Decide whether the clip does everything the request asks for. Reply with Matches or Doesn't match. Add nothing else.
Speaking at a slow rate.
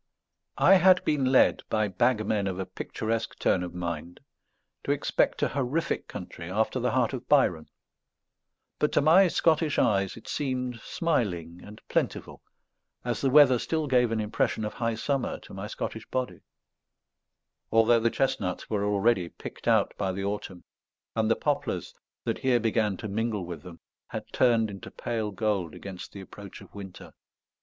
Doesn't match